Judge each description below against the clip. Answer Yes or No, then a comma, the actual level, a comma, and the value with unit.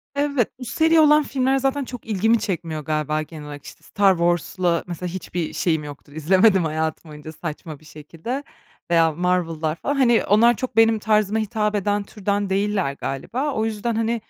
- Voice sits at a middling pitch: No, high, 195 Hz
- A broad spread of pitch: Yes, wide, 6.1 semitones